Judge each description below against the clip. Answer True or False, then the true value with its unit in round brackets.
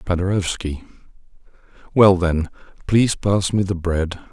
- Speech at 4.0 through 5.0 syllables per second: True (4.5 syllables/s)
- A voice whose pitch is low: True (90 Hz)